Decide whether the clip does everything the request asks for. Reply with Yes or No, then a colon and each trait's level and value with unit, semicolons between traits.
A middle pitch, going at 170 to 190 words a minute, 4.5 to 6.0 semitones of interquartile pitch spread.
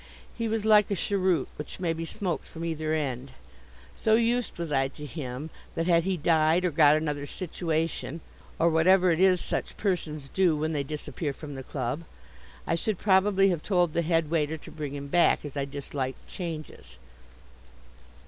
No: medium, 165 Hz; average, 180 wpm; average, 3.7 semitones